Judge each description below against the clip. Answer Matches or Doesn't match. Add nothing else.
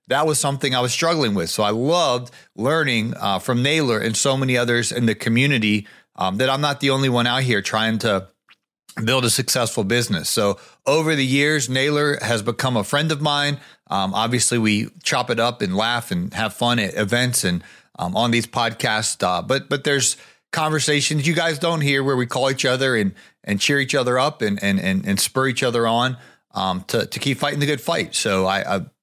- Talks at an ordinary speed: Doesn't match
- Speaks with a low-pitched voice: Matches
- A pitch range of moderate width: Matches